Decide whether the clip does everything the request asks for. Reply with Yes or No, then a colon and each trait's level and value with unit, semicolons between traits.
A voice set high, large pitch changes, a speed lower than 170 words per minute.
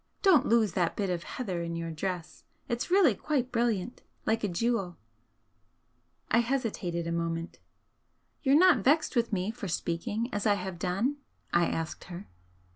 Yes: high, 205 Hz; wide, 5.8 semitones; average, 160 wpm